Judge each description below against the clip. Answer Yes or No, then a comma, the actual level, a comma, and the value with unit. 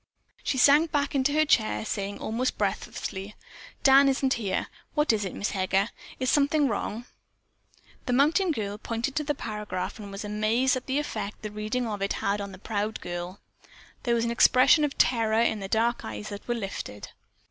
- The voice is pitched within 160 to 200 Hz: No, high, 225 Hz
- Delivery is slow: No, average, 190 wpm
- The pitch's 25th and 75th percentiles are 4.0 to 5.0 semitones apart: Yes, average, 4.6 semitones